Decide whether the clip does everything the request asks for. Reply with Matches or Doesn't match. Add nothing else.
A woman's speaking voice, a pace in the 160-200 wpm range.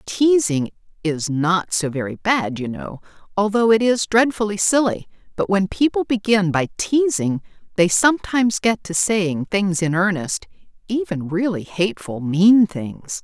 Doesn't match